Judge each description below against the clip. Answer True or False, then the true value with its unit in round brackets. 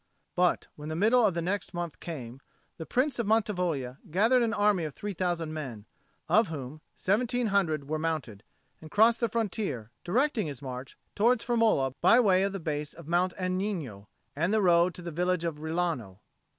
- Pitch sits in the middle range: True (175 Hz)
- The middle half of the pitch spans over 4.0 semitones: True (5.4 semitones)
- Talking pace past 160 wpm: True (185 wpm)